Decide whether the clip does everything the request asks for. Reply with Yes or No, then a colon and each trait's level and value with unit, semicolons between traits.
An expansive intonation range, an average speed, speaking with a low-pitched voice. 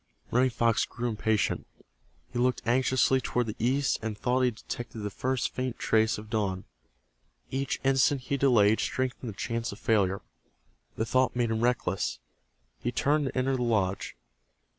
No: average, 2.9 semitones; average, 160 wpm; low, 120 Hz